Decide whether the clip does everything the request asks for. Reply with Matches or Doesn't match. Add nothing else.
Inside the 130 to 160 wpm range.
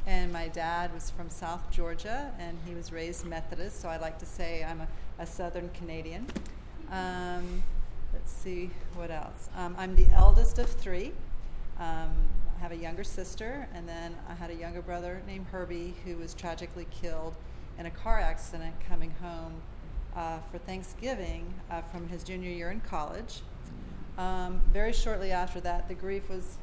Doesn't match